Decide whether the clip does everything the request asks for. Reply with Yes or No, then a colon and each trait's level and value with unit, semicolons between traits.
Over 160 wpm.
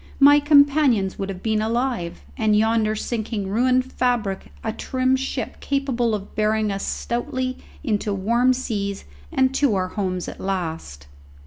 No: average, 145 wpm